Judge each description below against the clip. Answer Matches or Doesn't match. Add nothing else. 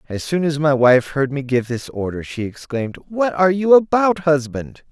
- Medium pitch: Matches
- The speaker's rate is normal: Doesn't match